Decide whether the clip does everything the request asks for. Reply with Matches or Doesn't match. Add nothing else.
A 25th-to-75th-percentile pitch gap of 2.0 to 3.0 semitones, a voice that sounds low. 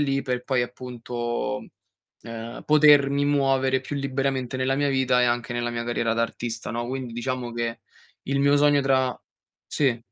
Matches